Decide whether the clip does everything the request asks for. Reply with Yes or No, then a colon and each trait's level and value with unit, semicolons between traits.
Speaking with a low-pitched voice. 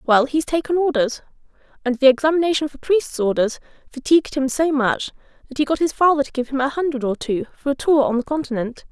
No: very high, 280 Hz